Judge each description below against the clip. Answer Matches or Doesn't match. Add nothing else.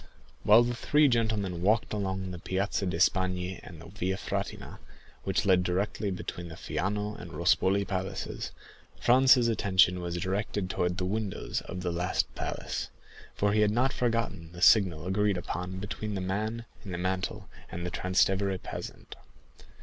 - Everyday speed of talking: Matches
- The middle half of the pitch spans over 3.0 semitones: Doesn't match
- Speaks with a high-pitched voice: Doesn't match